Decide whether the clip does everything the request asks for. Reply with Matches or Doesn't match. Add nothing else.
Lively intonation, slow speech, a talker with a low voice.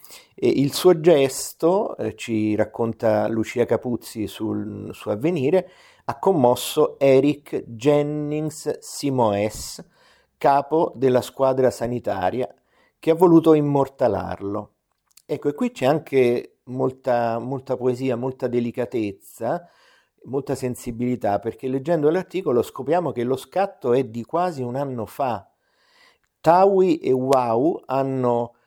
Doesn't match